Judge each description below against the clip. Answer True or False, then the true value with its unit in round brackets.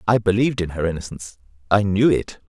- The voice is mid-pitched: False (100 Hz)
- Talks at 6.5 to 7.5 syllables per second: True (6.6 syllables/s)